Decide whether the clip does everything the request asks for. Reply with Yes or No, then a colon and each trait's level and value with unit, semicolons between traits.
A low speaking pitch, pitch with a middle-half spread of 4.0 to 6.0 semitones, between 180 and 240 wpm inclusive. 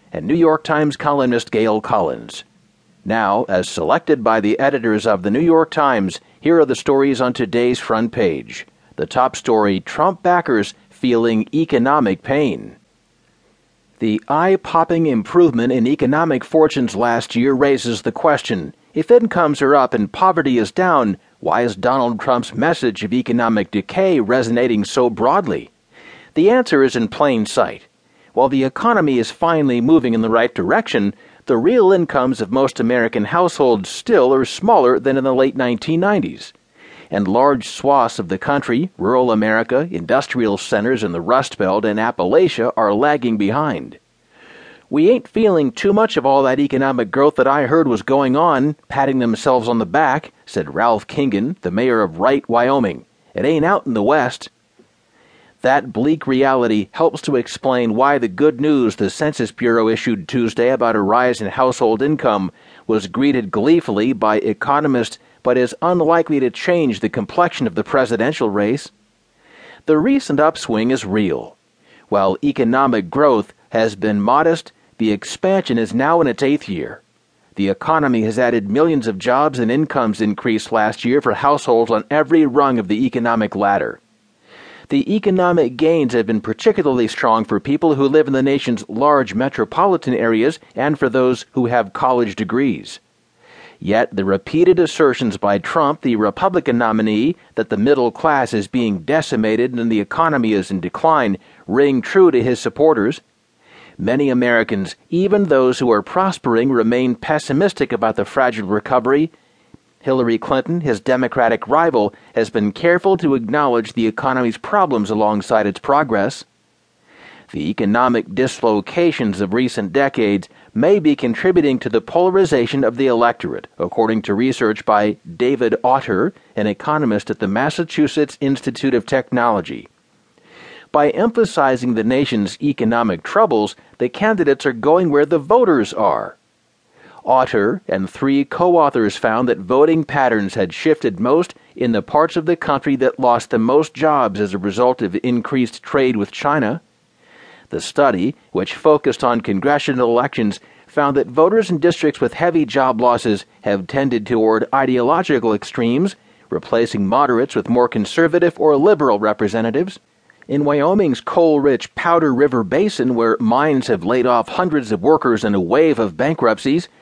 No: low, 130 Hz; average, 5.2 semitones; average, 155 wpm